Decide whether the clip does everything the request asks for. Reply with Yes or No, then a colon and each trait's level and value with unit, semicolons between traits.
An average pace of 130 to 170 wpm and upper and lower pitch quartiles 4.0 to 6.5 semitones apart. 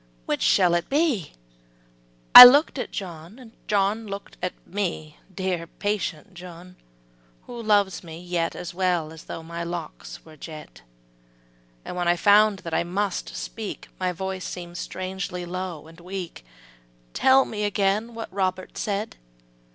No: average, 145 wpm; average, 3.1 semitones